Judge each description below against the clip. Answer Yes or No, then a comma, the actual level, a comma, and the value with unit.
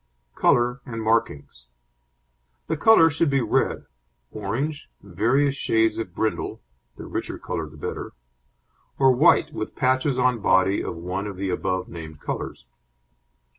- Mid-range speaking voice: No, low, 110 Hz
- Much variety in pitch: Yes, wide, 6.1 semitones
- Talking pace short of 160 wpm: Yes, slow, 135 wpm